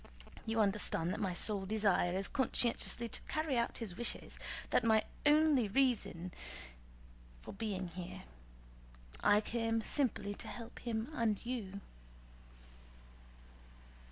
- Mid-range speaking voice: No, high, 220 Hz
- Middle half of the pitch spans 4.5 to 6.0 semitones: No, average, 3.3 semitones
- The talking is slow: Yes, slow, 125 wpm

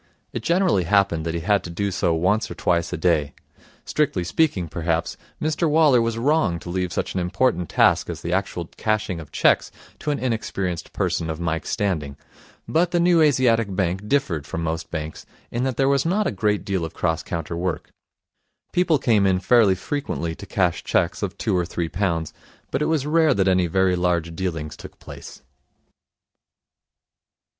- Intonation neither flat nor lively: No, wide, 6.9 semitones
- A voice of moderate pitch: No, very low, 95 Hz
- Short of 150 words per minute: No, average, 185 wpm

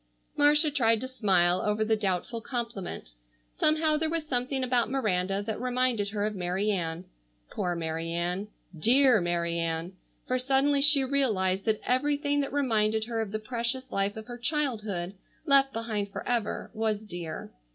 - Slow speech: No, average, 160 wpm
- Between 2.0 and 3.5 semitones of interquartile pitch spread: No, wide, 5.4 semitones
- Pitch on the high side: Yes, high, 220 Hz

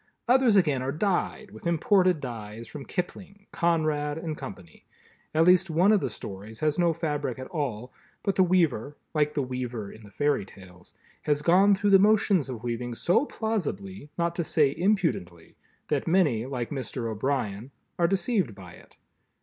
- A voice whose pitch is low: No, medium, 150 Hz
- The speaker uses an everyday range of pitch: No, wide, 7.2 semitones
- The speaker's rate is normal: Yes, average, 165 wpm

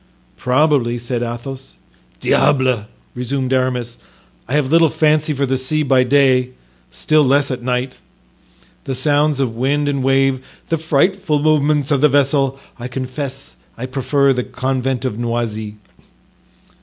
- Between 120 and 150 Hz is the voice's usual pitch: Yes, low, 135 Hz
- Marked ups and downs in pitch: No, narrow, 2.4 semitones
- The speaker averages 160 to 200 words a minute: No, average, 140 wpm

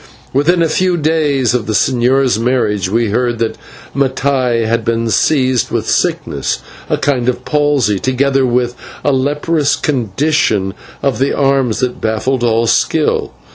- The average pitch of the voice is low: Yes, low, 130 Hz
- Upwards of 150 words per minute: No, average, 145 wpm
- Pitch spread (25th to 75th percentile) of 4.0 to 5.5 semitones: No, average, 3.3 semitones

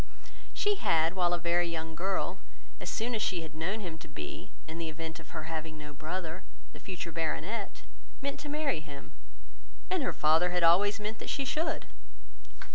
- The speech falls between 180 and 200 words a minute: Yes, average, 190 wpm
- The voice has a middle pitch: Yes, medium, 170 Hz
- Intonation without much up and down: No, average, 4.2 semitones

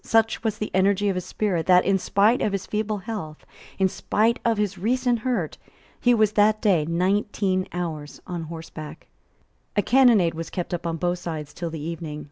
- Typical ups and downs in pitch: Yes, average, 4.2 semitones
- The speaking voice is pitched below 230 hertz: Yes, high, 190 Hz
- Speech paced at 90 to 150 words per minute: No, average, 190 wpm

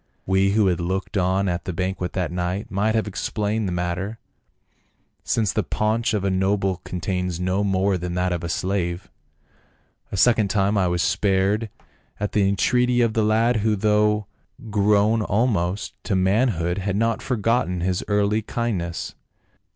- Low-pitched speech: Yes, low, 100 Hz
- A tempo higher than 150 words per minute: Yes, average, 160 wpm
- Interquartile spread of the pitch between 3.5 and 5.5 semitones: No, average, 2.7 semitones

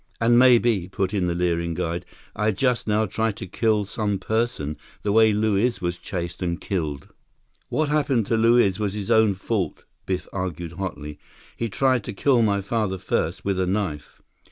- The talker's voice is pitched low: Yes, low, 100 Hz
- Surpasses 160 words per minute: Yes, average, 180 wpm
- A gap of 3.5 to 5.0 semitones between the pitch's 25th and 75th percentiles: Yes, average, 4.0 semitones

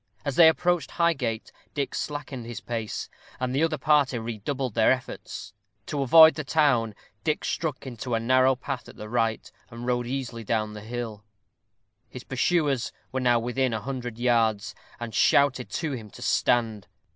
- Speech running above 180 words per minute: No, average, 170 wpm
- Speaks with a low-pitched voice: Yes, low, 125 Hz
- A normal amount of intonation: Yes, average, 3.5 semitones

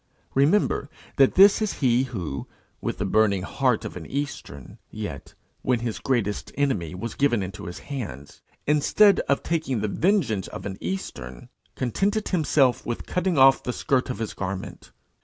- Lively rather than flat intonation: Yes, wide, 6.6 semitones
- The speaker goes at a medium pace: Yes, average, 160 wpm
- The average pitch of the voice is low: Yes, low, 125 Hz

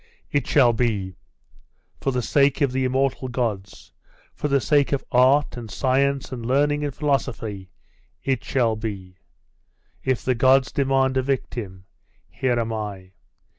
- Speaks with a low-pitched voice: Yes, low, 130 Hz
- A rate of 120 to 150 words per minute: Yes, average, 145 wpm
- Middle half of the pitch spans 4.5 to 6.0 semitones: No, average, 3.4 semitones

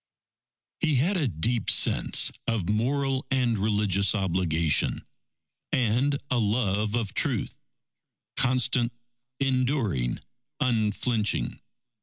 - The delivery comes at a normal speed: No, slow, 90 wpm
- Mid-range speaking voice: No, low, 115 Hz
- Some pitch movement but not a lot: Yes, average, 4.1 semitones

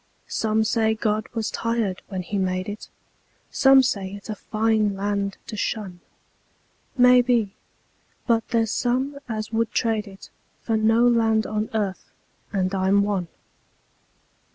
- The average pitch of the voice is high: Yes, high, 215 Hz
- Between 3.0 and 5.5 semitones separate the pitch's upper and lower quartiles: No, narrow, 2.4 semitones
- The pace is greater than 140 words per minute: No, slow, 135 wpm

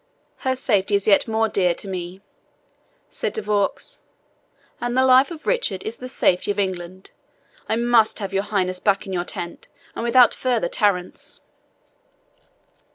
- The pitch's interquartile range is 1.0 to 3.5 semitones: No, average, 4.2 semitones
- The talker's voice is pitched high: Yes, high, 205 Hz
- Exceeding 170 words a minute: No, average, 160 wpm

